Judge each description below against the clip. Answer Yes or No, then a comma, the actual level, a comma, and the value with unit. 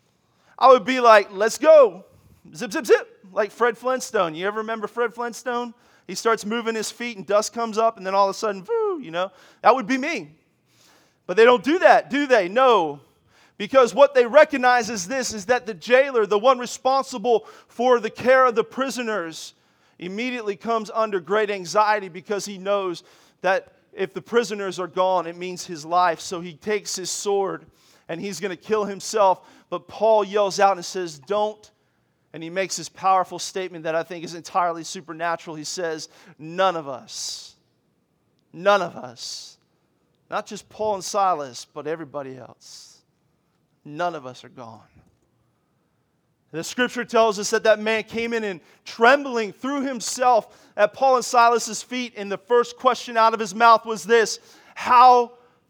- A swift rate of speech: No, average, 175 wpm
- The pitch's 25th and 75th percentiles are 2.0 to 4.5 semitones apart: No, average, 5.1 semitones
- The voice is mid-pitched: No, high, 210 Hz